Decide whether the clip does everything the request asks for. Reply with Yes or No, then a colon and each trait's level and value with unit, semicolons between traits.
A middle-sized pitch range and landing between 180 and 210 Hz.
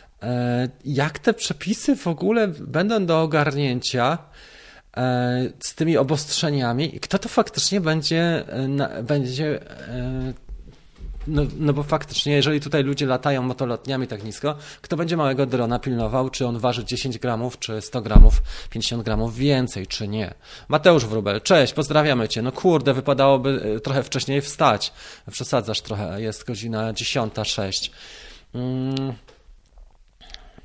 No: average, 3.9 semitones; low, 135 Hz